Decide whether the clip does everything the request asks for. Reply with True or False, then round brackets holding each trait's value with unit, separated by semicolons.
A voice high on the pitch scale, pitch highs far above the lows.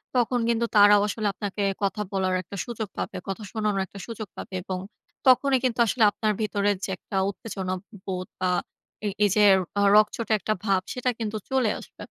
False (210 Hz; 2.6 semitones)